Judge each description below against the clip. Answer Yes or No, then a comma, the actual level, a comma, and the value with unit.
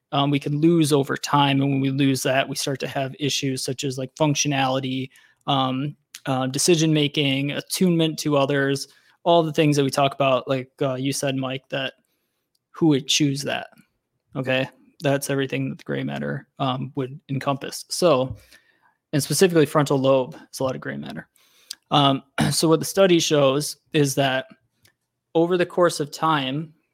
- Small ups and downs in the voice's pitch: Yes, narrow, 2.1 semitones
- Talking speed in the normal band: Yes, average, 170 wpm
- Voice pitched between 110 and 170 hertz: Yes, medium, 140 Hz